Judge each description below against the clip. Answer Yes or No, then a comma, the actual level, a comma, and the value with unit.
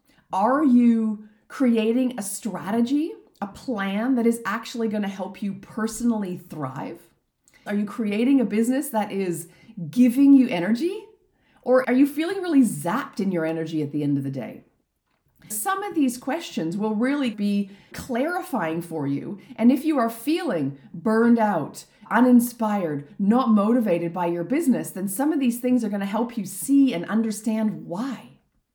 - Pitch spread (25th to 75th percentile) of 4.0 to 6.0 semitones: Yes, average, 4.6 semitones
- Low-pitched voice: No, high, 225 Hz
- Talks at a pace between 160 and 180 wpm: Yes, average, 165 wpm